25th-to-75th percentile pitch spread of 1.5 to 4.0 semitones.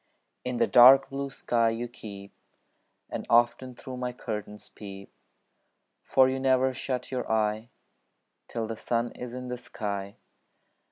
Yes: average, 2.7 semitones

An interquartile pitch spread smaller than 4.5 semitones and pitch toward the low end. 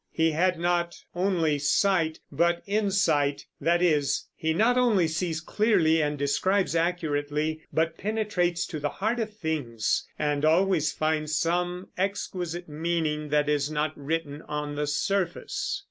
No: average, 3.4 semitones; medium, 165 Hz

